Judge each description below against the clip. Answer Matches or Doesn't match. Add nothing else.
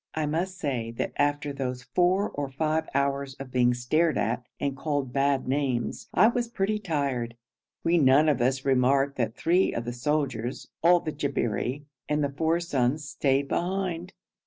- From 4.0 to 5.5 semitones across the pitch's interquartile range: Doesn't match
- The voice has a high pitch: Doesn't match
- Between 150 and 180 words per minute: Matches